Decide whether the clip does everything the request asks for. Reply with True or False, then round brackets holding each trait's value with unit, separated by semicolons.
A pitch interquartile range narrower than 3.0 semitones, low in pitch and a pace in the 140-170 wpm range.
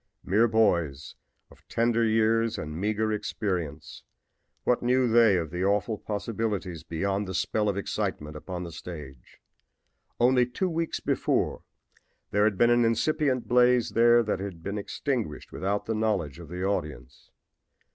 False (4.9 semitones; 105 Hz; 145 wpm)